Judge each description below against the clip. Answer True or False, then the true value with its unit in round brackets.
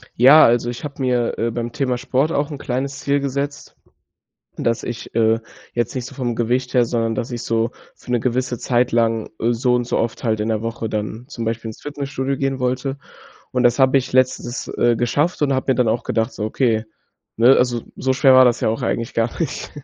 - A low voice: True (125 Hz)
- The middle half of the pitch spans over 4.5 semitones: False (2.4 semitones)